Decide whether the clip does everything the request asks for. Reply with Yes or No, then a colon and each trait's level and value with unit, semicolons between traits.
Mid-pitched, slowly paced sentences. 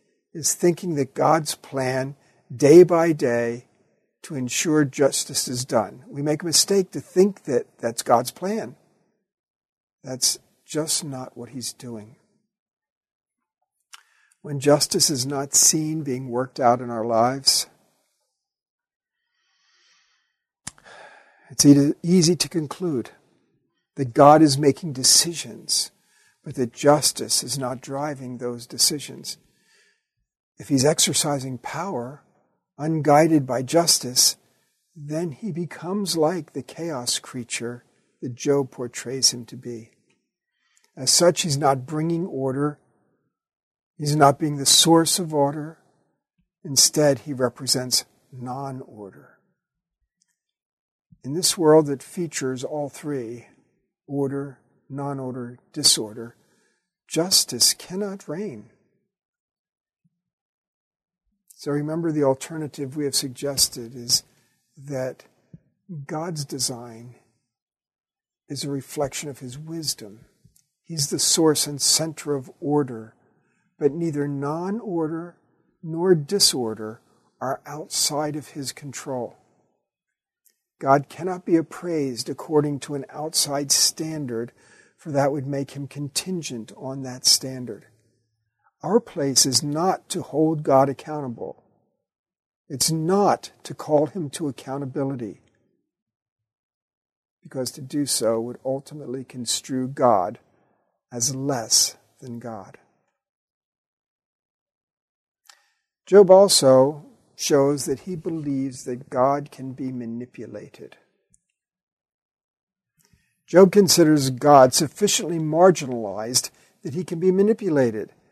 Yes: medium, 145 Hz; slow, 105 wpm